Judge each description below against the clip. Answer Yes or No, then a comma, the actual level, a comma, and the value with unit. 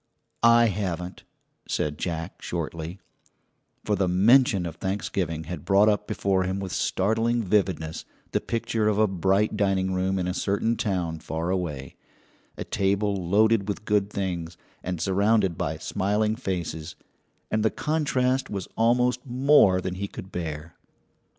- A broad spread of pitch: No, average, 3.3 semitones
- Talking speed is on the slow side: No, average, 145 wpm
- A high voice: No, very low, 95 Hz